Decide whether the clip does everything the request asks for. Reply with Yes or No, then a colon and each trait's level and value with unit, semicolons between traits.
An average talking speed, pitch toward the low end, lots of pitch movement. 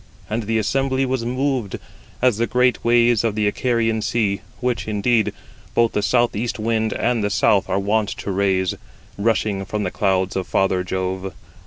No: average, 185 wpm; low, 110 Hz; average, 3.2 semitones